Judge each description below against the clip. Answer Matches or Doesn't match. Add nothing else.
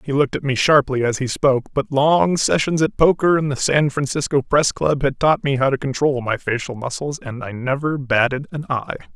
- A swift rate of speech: Matches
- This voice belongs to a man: Matches